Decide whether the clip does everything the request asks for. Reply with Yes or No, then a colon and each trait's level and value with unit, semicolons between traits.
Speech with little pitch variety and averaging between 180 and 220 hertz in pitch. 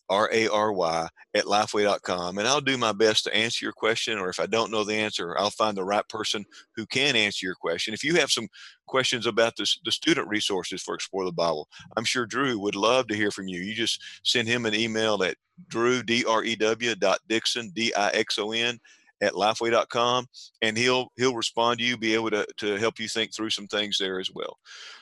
No: narrow, 2.1 semitones; low, 110 Hz